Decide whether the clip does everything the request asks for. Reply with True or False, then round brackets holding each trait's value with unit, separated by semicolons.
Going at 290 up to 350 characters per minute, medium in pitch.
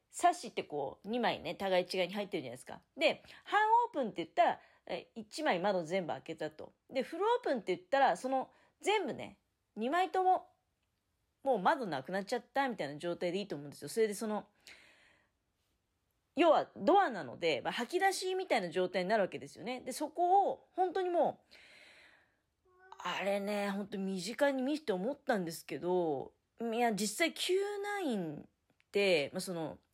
False (345 characters per minute; 230 Hz)